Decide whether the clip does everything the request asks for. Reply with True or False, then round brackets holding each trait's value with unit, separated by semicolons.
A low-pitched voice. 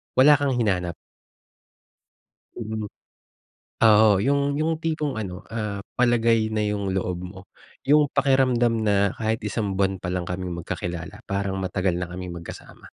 True (105 Hz)